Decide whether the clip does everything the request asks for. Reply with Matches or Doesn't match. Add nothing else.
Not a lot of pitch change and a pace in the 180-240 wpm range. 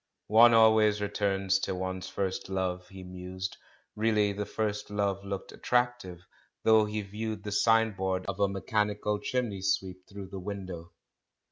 Doesn't match